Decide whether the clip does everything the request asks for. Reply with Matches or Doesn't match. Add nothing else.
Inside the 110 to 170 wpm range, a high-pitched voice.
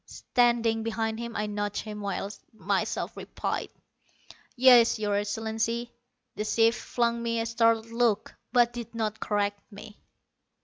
Matches